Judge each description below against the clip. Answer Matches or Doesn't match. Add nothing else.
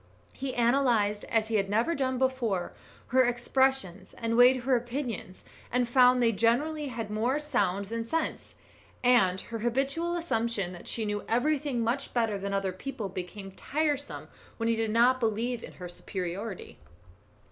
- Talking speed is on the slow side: Doesn't match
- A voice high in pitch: Matches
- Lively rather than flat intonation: Doesn't match